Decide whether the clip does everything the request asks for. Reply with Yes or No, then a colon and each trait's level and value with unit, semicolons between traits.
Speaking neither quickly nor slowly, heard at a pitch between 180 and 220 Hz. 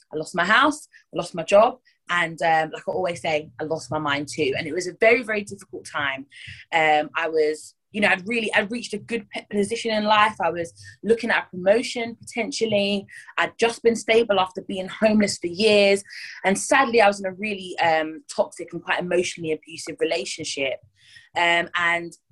Yes: average, 195 wpm; high, 190 Hz